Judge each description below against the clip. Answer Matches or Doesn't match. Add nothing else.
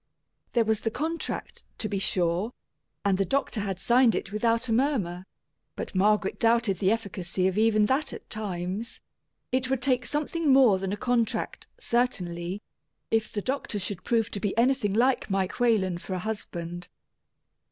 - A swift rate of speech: Doesn't match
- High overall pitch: Matches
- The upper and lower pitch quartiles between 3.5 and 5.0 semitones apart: Matches